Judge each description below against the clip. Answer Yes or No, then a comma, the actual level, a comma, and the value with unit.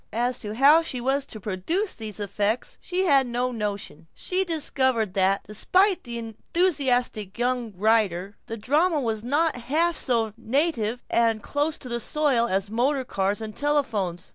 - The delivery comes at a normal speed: Yes, average, 160 wpm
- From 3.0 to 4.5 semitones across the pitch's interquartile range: No, average, 5.3 semitones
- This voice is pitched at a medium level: No, high, 240 Hz